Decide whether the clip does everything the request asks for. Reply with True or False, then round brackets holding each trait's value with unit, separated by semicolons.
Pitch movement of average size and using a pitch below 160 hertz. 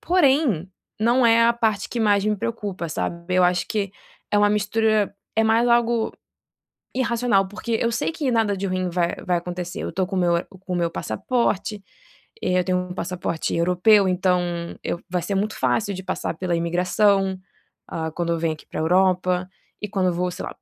False (3.6 semitones; 190 Hz)